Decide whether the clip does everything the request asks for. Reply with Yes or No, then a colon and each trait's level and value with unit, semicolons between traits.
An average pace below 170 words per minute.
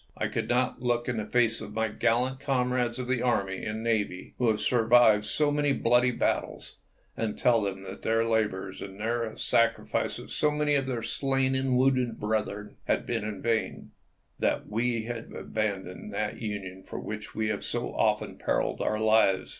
No: average, 185 wpm